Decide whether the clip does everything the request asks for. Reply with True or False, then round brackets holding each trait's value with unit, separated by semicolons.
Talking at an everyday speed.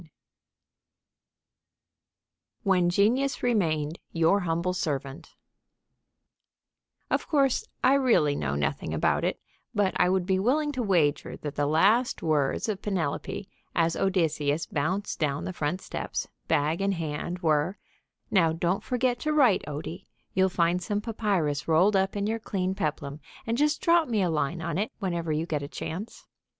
True (155 wpm)